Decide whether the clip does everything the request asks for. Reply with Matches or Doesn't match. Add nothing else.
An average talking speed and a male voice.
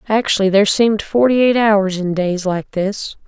Doesn't match